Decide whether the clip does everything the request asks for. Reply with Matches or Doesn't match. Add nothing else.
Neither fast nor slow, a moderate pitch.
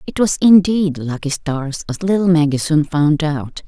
Matches